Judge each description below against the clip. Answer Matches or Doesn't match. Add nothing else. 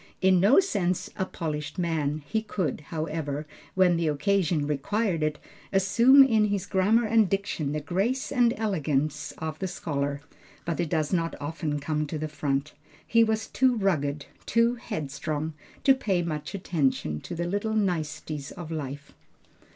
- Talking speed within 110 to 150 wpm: Doesn't match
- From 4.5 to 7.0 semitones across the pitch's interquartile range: Matches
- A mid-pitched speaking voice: Matches